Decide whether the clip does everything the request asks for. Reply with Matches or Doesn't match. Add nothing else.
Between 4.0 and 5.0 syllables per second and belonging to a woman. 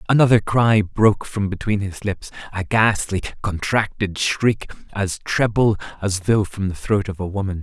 Doesn't match